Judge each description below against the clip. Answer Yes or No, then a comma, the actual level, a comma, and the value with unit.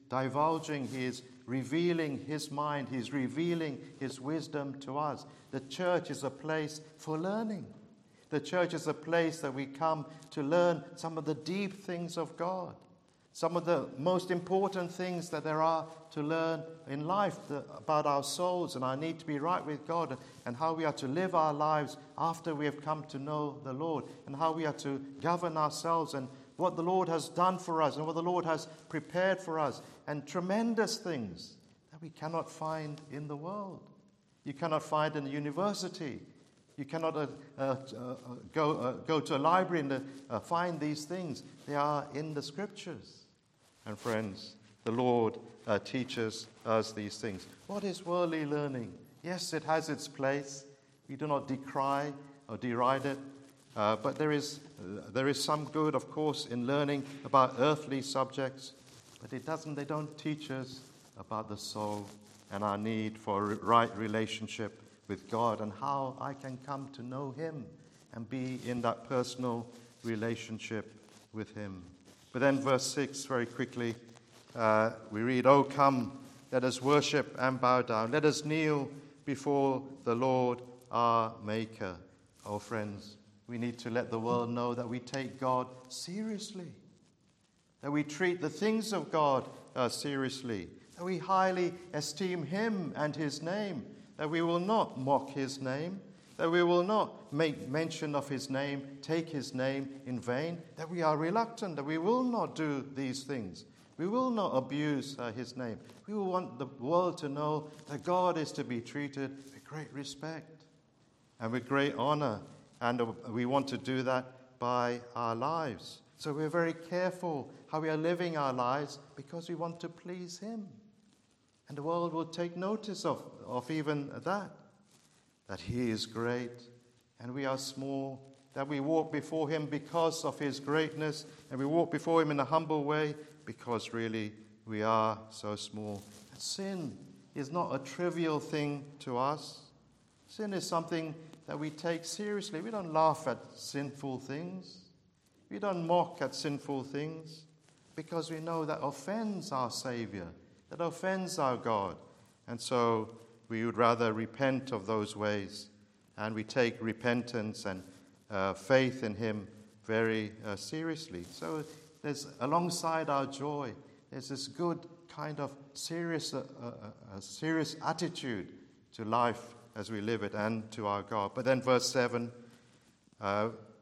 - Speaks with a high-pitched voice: No, medium, 140 Hz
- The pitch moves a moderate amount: Yes, average, 4.7 semitones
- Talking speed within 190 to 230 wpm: No, average, 165 wpm